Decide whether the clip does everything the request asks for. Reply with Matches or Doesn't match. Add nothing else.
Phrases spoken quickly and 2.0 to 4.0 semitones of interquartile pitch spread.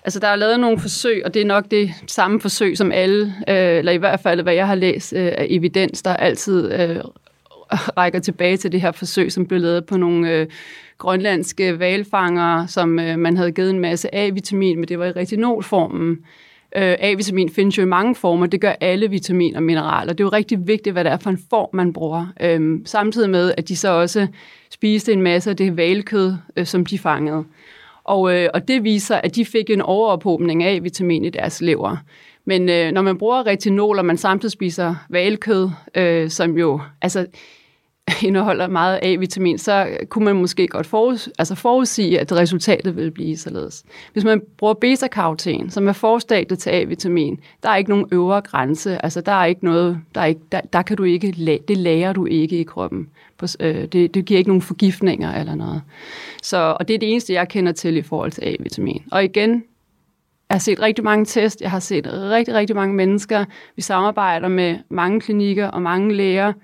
Doesn't match